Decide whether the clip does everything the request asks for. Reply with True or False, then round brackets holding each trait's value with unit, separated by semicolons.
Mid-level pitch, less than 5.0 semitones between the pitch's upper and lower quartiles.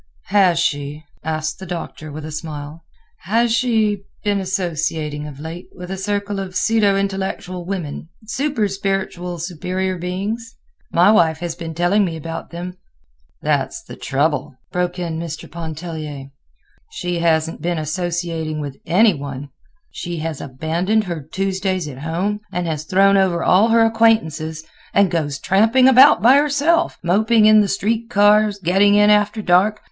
True (180 Hz; 4.3 semitones)